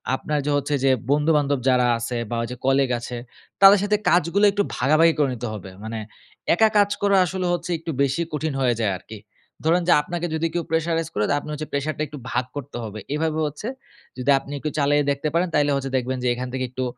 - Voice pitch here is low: No, medium, 145 Hz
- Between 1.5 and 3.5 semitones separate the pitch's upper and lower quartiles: No, average, 4.2 semitones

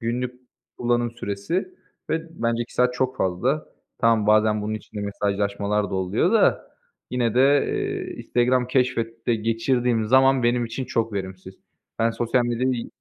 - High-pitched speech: No, low, 120 Hz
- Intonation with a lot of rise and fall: No, average, 3.1 semitones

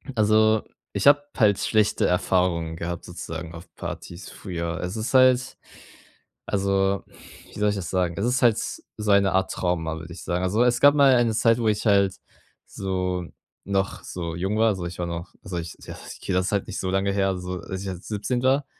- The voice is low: Yes, very low, 95 Hz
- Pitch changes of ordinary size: Yes, average, 3.4 semitones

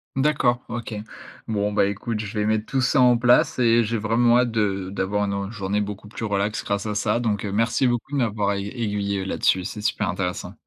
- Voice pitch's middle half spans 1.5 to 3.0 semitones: Yes, average, 2.7 semitones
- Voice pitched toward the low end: Yes, low, 105 Hz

